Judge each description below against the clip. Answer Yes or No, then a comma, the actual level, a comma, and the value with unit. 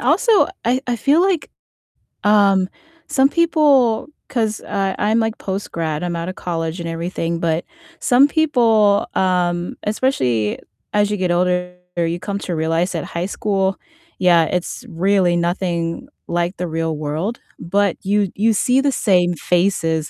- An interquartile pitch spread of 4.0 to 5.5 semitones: Yes, average, 4.4 semitones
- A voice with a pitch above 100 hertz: Yes, high, 190 Hz